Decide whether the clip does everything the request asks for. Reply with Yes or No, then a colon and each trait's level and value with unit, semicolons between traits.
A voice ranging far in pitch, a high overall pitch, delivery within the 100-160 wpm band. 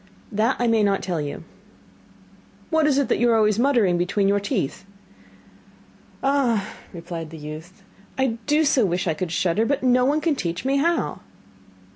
No: wide, 7.0 semitones; high, 215 Hz; average, 175 wpm